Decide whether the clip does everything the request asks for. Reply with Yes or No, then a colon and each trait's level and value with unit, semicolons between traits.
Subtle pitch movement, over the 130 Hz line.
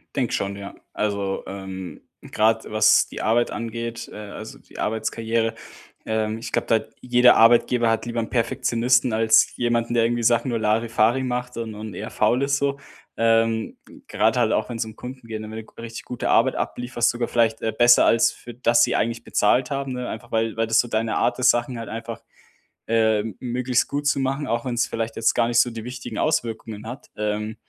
No: narrow, 1.6 semitones; low, 115 Hz